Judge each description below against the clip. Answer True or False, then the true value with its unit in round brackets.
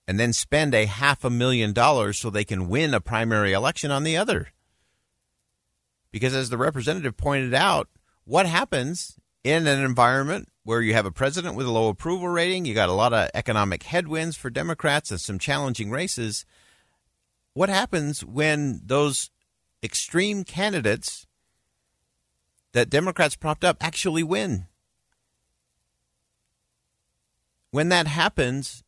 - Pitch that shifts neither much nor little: False (6.8 semitones)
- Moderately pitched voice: False (130 Hz)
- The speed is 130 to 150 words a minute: True (140 wpm)